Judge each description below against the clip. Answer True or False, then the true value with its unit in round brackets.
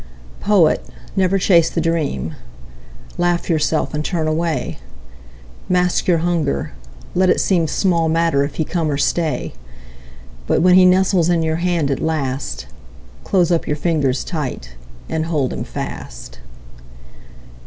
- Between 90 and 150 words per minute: True (140 wpm)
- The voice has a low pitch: False (165 Hz)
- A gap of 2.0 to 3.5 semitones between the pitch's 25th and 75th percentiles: True (2.7 semitones)